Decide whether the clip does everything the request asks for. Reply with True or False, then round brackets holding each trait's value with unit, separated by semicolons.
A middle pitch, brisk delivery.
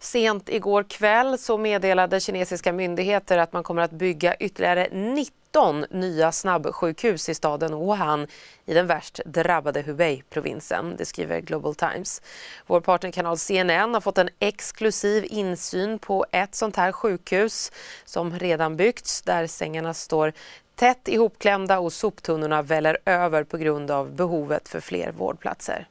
False (180 Hz; 140 wpm)